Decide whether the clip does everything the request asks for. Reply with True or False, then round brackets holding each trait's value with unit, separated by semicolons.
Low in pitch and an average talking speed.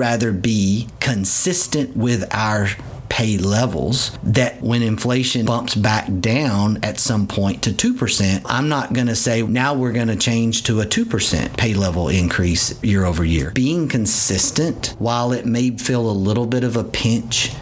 True (115 Hz; 160 wpm)